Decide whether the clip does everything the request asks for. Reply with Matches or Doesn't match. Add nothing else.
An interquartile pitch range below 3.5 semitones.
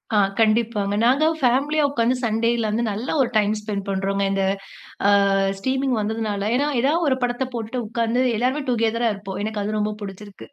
Matches